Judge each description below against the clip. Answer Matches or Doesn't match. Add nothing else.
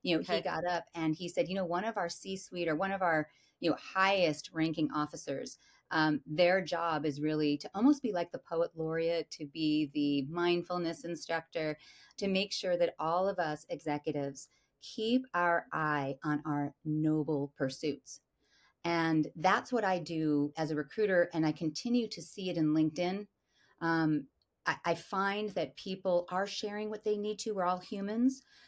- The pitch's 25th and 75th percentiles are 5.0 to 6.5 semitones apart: Doesn't match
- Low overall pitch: Doesn't match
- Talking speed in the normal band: Matches